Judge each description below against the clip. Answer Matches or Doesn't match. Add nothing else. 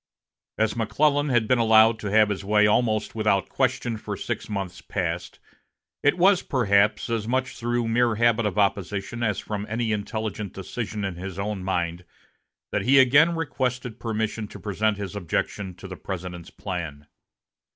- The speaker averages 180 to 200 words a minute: Doesn't match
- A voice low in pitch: Matches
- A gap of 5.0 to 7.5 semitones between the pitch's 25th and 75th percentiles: Doesn't match